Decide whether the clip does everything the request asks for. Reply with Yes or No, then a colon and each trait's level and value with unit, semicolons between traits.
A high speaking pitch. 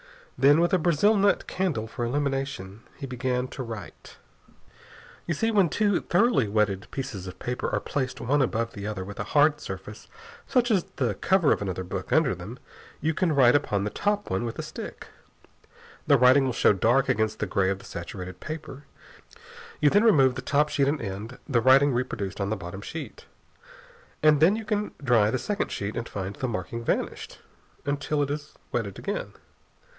No: low, 130 Hz